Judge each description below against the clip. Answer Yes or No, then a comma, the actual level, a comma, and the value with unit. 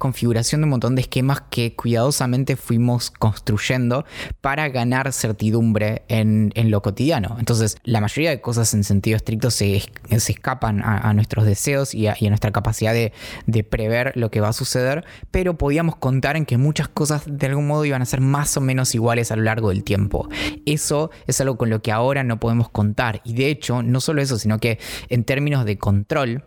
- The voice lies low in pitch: Yes, low, 120 Hz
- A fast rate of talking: Yes, fast, 205 wpm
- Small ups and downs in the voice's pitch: No, average, 3.7 semitones